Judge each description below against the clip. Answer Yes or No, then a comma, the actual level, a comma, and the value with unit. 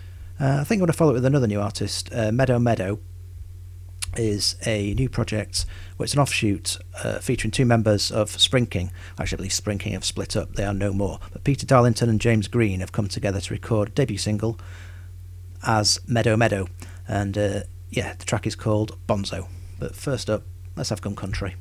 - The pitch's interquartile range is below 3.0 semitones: No, average, 3.7 semitones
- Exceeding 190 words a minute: Yes, average, 200 wpm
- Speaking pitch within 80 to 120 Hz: Yes, low, 100 Hz